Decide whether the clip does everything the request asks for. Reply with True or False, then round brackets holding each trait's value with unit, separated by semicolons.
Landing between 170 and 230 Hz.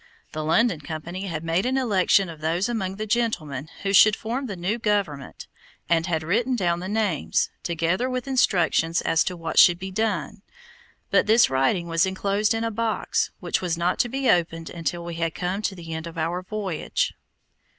True (185 Hz)